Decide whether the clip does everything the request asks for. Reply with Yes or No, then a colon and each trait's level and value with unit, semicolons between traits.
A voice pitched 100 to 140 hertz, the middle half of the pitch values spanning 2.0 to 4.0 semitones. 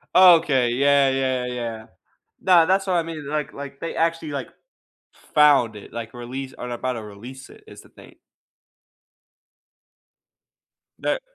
No: low, 135 Hz; average, 4.9 semitones